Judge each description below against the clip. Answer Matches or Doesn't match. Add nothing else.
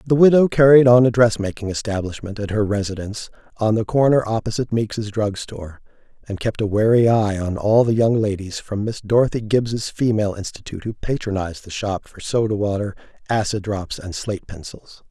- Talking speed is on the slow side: Doesn't match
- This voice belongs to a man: Matches